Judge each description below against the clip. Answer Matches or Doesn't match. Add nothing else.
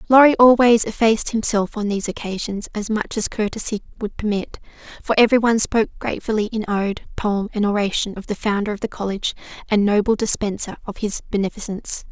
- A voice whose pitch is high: Matches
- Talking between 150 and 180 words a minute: Matches